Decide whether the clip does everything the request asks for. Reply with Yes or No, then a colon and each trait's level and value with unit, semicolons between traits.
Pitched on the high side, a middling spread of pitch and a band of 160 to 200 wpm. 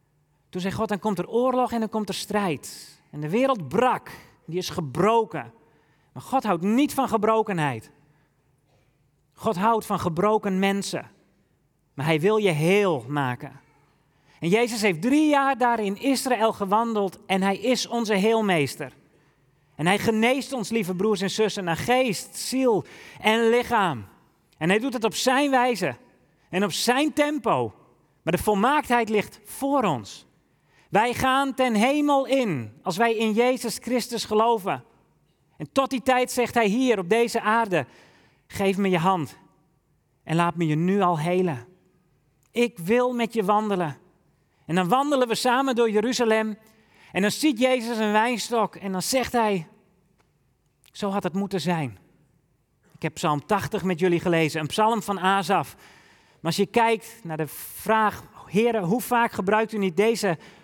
No: high, 200 Hz; wide, 6.4 semitones; average, 165 wpm